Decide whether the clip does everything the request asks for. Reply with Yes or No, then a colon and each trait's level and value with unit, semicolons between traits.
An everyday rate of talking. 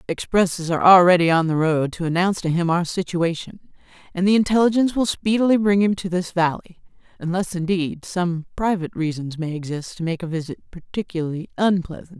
Yes: average, 170 wpm